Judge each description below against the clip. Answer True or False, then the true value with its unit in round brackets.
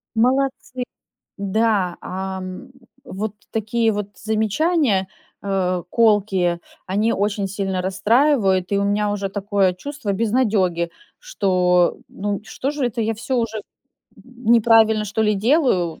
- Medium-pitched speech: False (210 Hz)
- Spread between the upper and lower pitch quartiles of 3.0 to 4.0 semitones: True (3.3 semitones)